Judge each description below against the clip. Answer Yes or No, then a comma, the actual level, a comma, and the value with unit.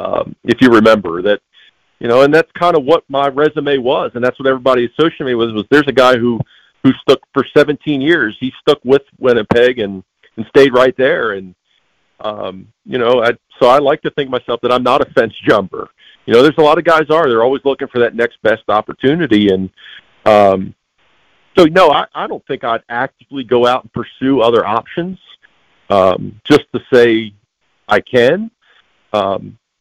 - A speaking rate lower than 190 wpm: No, average, 195 wpm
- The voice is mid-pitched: No, low, 130 Hz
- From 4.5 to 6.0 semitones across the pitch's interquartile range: No, average, 3.8 semitones